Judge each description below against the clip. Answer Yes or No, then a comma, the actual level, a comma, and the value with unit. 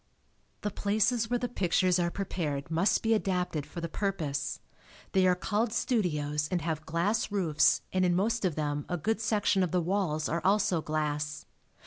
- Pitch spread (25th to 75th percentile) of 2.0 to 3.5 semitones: No, average, 4.8 semitones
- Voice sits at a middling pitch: Yes, medium, 180 Hz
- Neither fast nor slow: Yes, average, 175 wpm